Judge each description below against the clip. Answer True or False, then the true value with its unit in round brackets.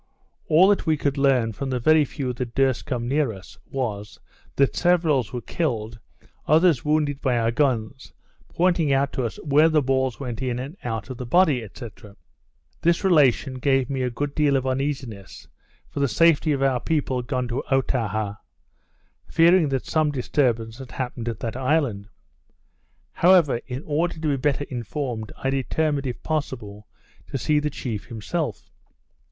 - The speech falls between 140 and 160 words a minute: False (170 wpm)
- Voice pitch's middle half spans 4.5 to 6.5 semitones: False (3.8 semitones)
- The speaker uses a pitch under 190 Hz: True (135 Hz)